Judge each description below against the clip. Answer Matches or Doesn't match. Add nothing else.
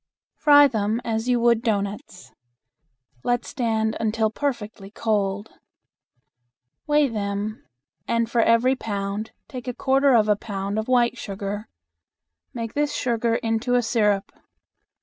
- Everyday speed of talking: Doesn't match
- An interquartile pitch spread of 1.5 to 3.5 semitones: Matches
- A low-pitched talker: Doesn't match